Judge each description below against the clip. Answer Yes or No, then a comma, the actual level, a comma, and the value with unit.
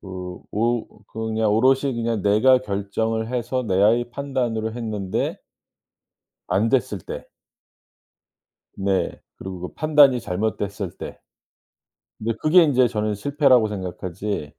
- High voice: No, low, 110 Hz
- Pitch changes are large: No, average, 3.8 semitones